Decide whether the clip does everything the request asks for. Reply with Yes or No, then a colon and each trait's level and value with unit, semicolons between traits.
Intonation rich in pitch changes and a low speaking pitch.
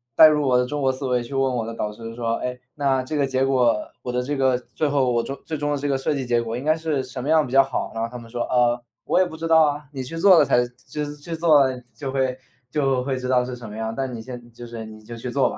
No: average, 3.1 semitones; low, 130 Hz